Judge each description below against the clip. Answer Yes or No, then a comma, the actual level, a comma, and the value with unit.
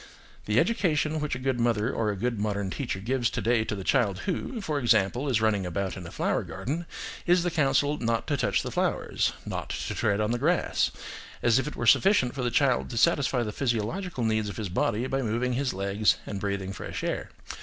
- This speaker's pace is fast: Yes, fast, 220 wpm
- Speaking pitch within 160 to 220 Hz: No, low, 120 Hz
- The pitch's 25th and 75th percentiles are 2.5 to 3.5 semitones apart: No, average, 5.0 semitones